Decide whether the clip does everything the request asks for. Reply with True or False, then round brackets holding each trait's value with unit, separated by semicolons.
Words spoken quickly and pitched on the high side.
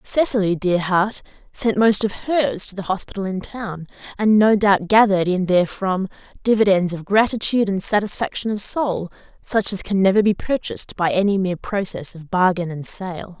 False (175 wpm; 195 Hz)